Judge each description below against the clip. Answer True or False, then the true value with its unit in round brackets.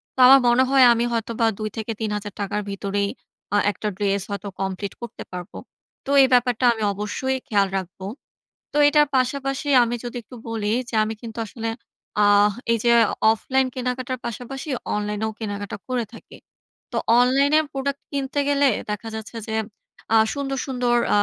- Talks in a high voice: True (230 Hz)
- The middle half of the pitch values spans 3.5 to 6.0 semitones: True (4.0 semitones)